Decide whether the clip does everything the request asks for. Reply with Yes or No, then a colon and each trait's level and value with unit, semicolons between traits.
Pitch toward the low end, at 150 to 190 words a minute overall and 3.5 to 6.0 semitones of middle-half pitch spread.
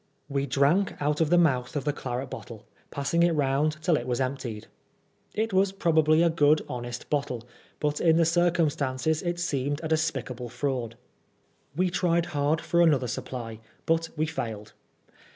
No: medium, 150 Hz; average, 165 wpm; average, 4.3 semitones